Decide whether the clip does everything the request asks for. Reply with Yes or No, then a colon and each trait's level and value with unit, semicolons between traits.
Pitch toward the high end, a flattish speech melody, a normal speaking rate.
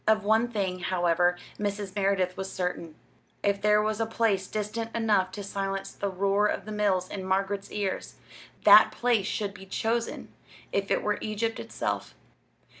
Yes: high, 200 Hz; narrow, 2.0 semitones; average, 165 wpm